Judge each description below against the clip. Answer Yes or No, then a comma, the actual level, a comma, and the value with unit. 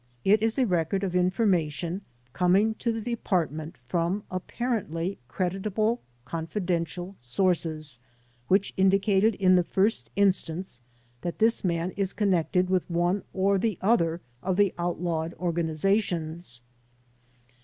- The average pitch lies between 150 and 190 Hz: Yes, medium, 185 Hz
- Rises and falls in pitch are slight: No, average, 3.0 semitones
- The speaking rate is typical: No, slow, 120 wpm